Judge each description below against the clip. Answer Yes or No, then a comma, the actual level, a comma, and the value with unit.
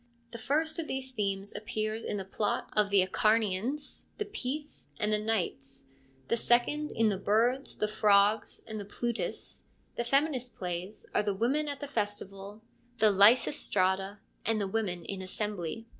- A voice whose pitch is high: Yes, high, 215 Hz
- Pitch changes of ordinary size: Yes, average, 3.6 semitones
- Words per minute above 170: No, average, 160 wpm